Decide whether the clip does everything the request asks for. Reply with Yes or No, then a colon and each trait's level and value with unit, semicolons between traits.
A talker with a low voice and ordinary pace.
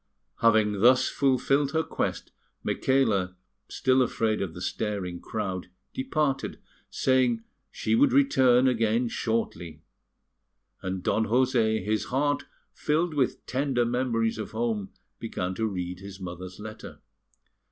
No: low, 115 Hz; slow, 120 wpm